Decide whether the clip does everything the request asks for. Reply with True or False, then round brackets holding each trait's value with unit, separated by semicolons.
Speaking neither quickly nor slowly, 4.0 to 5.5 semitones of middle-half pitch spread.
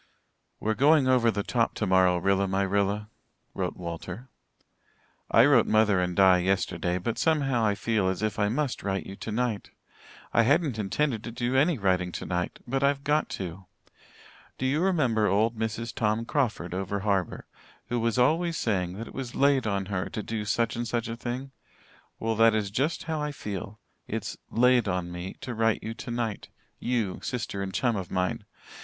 True (180 wpm; 4.3 semitones)